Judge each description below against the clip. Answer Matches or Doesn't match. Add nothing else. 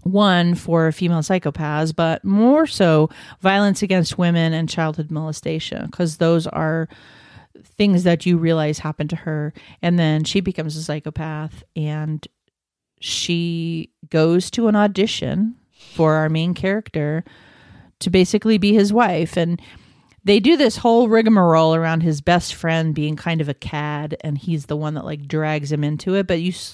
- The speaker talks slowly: Doesn't match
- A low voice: Doesn't match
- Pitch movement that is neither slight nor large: Matches